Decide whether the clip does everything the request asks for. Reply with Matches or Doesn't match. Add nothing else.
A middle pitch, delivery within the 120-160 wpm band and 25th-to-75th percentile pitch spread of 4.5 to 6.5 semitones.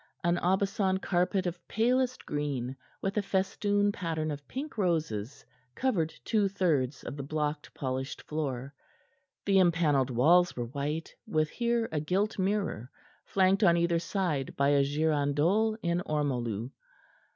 Matches